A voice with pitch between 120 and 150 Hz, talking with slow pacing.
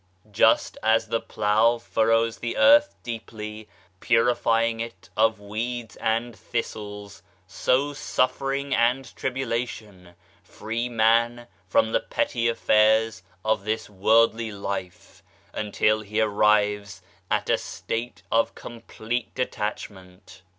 No: low, 110 Hz; slow, 110 wpm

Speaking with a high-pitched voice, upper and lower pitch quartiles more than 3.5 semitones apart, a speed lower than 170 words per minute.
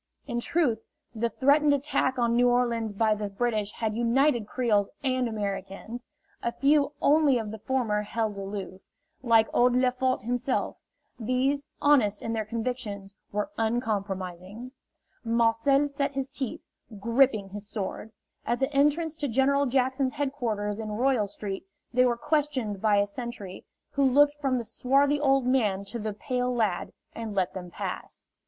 Yes: high, 240 Hz; average, 4.2 semitones; average, 155 wpm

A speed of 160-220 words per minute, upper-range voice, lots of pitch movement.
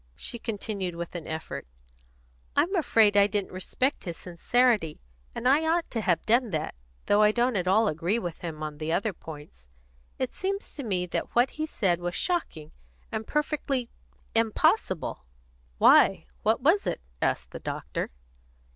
Yes: average, 165 wpm; high, 205 Hz; wide, 6.6 semitones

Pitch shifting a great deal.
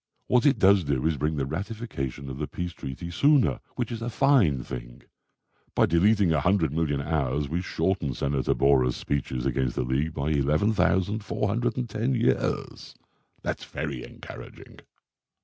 Yes: wide, 7.2 semitones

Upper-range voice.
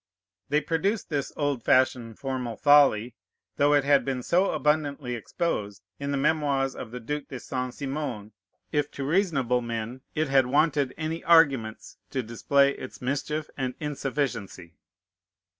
No: medium, 140 Hz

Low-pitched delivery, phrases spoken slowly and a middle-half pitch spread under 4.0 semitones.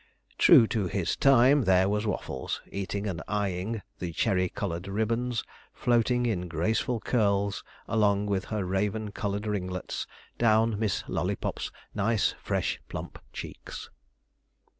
Yes: low, 105 Hz; slow, 125 wpm; average, 2.9 semitones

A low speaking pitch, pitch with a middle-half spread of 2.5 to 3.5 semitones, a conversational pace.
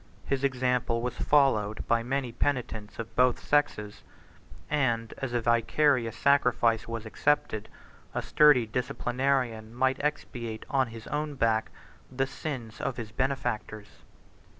No: low, 125 Hz; average, 3.2 semitones; slow, 125 wpm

